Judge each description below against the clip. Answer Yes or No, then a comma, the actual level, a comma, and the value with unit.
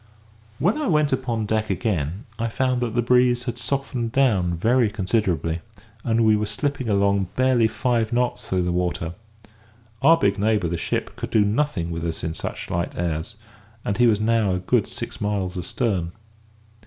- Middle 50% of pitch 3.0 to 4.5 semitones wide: No, average, 5.1 semitones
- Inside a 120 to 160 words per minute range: No, average, 180 wpm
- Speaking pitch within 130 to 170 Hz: No, low, 110 Hz